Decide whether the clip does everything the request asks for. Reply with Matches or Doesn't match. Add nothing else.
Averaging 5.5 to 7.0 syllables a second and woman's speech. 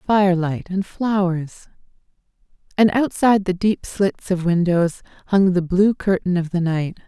Doesn't match